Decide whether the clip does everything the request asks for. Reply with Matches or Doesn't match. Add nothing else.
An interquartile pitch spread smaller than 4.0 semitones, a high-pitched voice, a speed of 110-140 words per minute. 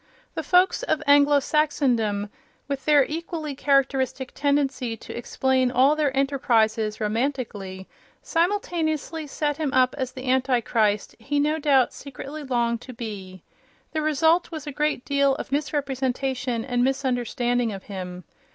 Matches